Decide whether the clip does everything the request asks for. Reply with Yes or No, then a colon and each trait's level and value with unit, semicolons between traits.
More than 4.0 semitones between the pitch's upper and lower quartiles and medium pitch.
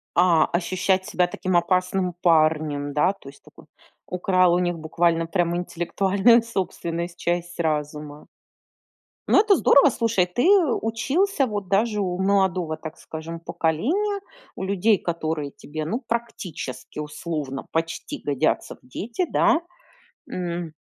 No: average, 3.7 semitones; medium, 175 Hz